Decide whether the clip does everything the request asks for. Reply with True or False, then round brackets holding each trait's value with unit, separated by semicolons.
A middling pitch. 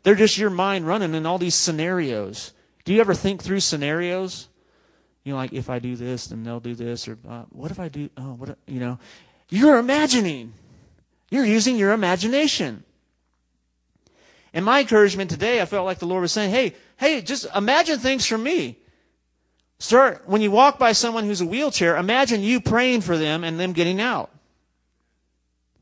True (180 Hz)